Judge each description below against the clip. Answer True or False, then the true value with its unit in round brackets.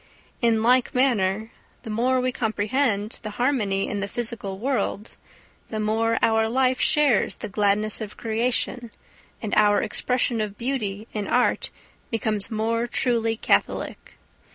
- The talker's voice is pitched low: False (225 Hz)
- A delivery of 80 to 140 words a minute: True (135 wpm)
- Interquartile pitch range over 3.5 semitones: False (2.7 semitones)